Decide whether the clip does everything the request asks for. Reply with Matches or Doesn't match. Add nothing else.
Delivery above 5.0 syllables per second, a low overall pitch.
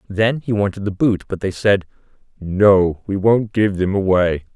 Doesn't match